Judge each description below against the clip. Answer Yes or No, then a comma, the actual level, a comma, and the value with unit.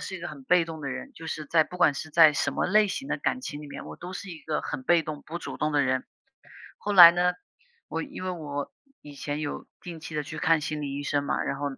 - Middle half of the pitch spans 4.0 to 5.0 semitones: No, average, 3.3 semitones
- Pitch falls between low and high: Yes, medium, 160 Hz